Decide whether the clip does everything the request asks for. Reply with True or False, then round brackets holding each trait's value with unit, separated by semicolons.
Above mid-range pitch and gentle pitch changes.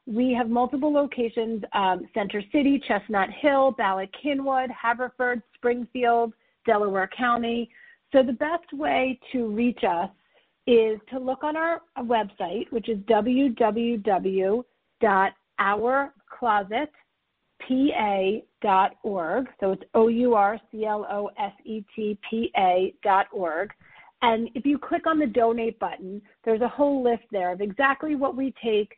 False (235 Hz; 3.9 semitones)